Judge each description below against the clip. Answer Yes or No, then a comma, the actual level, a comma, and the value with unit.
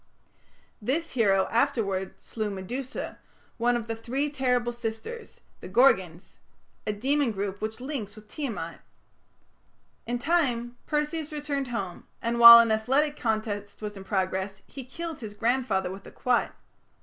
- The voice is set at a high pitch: Yes, high, 235 Hz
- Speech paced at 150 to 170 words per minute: No, average, 140 wpm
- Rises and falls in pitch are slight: No, average, 4.6 semitones